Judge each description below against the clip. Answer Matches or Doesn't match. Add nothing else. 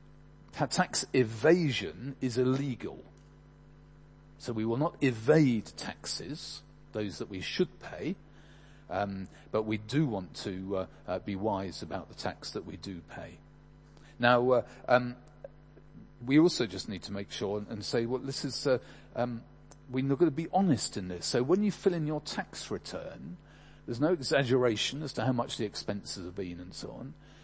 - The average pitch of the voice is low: Matches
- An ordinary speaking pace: Matches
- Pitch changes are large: Matches